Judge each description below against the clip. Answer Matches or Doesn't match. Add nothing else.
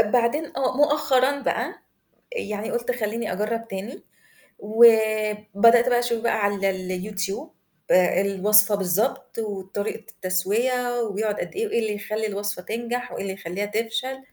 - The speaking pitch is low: Doesn't match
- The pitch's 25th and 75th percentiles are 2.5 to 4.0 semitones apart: Matches